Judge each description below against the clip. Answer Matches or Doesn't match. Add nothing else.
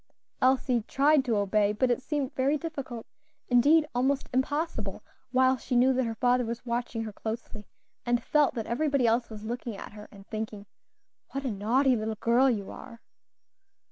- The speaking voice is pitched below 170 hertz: Doesn't match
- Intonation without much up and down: Doesn't match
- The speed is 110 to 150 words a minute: Doesn't match